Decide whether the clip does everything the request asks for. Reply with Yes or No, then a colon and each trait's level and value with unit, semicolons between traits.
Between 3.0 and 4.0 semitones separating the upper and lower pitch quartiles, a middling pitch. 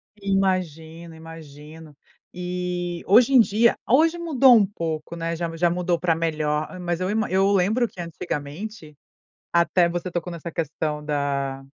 Yes: average, 3.4 semitones; medium, 170 Hz